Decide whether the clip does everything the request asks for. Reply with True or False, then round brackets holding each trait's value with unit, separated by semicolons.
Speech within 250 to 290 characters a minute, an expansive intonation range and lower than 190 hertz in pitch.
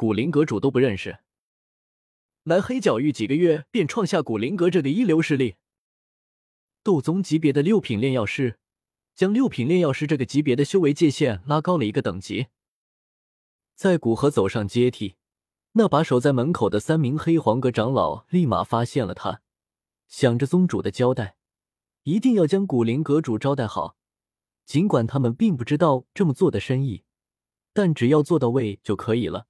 True (260 characters per minute; 6.6 semitones; 140 Hz)